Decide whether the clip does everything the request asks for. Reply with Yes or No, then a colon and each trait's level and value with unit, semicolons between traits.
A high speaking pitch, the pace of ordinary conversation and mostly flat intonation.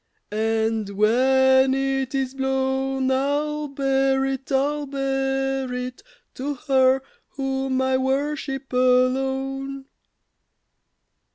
No: very high, 265 Hz; slow, 90 wpm; narrow, 0.7 semitones